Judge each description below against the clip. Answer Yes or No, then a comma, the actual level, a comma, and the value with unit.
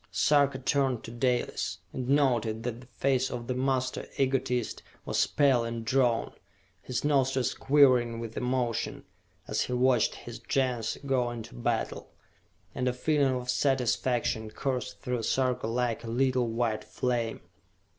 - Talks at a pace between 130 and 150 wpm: Yes, average, 145 wpm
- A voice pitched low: Yes, low, 125 Hz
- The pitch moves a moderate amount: No, narrow, 2.1 semitones